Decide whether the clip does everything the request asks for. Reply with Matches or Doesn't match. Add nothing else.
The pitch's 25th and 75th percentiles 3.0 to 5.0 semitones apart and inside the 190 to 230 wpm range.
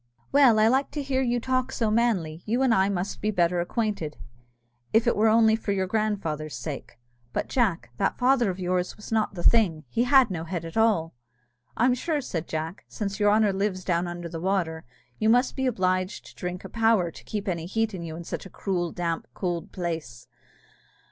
Matches